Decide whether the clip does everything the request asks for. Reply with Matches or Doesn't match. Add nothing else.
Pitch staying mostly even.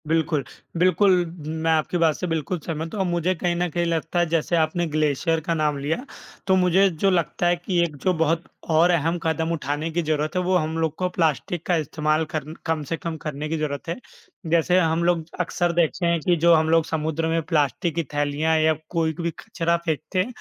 Matches